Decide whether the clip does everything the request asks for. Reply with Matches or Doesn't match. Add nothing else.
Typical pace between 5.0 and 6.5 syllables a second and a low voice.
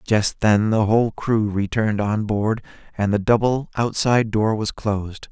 Doesn't match